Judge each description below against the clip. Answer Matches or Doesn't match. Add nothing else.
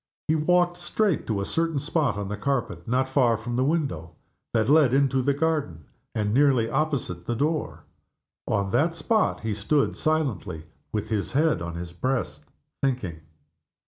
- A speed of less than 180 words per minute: Matches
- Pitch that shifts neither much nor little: Doesn't match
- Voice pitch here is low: Matches